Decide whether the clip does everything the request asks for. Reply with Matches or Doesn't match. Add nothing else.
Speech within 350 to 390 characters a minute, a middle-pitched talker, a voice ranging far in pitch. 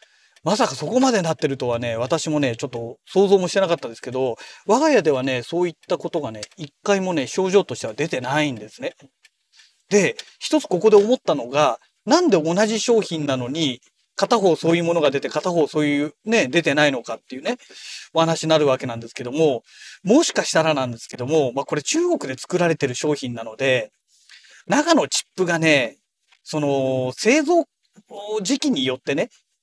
Matches